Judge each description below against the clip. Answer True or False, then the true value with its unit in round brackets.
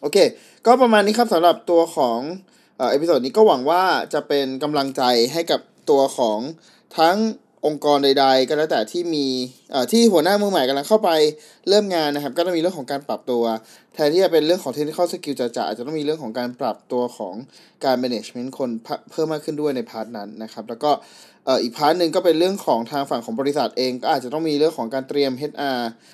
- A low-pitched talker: False (150 Hz)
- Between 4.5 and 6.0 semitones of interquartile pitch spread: True (5.0 semitones)